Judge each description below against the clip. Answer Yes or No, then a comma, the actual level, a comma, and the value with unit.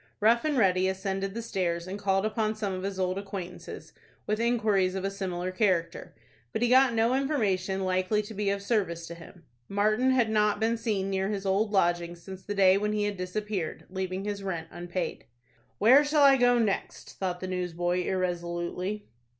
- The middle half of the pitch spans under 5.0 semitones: Yes, average, 2.7 semitones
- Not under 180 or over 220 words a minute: Yes, average, 190 wpm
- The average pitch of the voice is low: No, high, 195 Hz